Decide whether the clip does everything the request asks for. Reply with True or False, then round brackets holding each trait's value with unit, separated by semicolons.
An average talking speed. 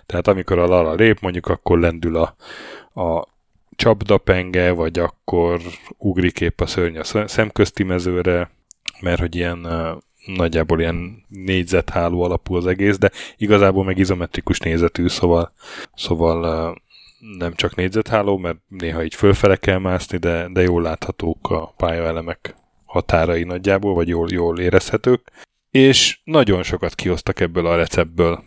True (135 wpm)